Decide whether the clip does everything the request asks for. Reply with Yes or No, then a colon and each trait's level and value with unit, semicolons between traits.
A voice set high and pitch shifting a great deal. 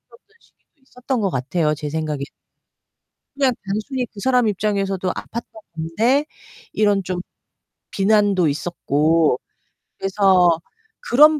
Yes: high, 195 Hz; wide, 6.2 semitones